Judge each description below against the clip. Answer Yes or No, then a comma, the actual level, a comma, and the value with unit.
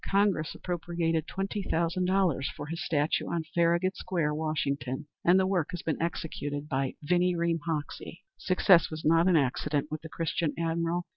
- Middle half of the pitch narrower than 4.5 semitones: Yes, narrow, 2.5 semitones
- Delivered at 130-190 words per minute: Yes, average, 165 wpm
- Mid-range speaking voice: Yes, medium, 165 Hz